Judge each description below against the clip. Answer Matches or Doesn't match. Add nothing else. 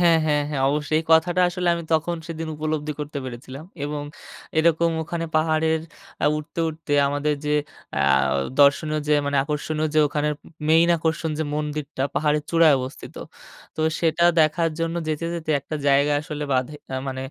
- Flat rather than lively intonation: Matches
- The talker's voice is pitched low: Doesn't match